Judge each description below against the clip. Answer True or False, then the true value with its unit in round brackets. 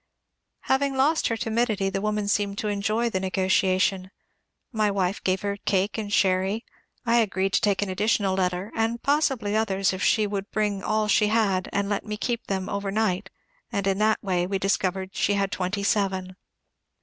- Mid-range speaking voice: False (200 Hz)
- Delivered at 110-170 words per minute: False (185 wpm)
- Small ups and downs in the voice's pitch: True (2.2 semitones)